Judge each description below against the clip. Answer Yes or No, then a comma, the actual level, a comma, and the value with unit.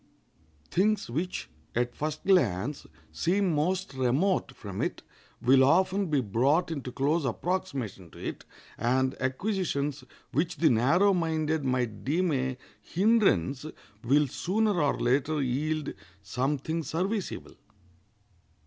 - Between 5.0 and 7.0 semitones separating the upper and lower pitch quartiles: Yes, wide, 5.6 semitones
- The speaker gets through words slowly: Yes, slow, 115 wpm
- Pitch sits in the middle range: Yes, medium, 150 Hz